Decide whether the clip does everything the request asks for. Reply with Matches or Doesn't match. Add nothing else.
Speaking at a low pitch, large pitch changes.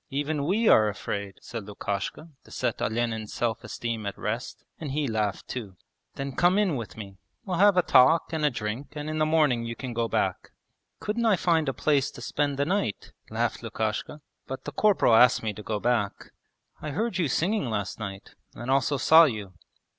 Matches